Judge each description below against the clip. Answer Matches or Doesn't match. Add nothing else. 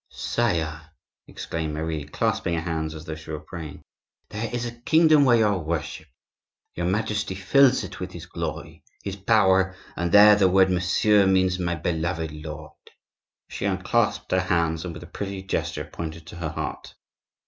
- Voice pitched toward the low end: Matches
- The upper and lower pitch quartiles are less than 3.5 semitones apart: Doesn't match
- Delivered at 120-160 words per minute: Doesn't match